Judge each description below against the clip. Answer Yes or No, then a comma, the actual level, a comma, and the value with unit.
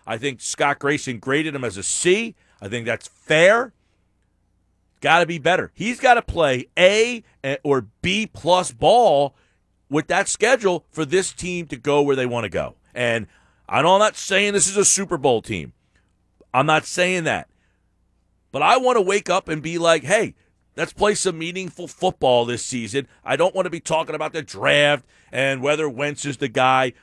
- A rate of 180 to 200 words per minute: Yes, average, 190 wpm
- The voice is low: No, medium, 145 Hz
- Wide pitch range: Yes, wide, 6.8 semitones